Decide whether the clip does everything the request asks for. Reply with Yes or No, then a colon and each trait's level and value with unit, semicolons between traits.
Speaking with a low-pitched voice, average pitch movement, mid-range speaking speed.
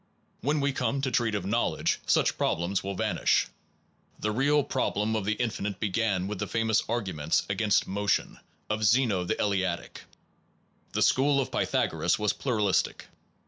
Yes: low, 105 Hz; average, 3.7 semitones; average, 155 wpm